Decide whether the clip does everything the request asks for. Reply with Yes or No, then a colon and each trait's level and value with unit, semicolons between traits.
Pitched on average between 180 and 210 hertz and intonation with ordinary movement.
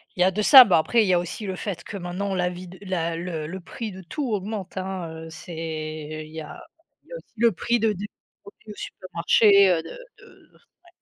Yes: medium, 185 Hz; average, 3.6 semitones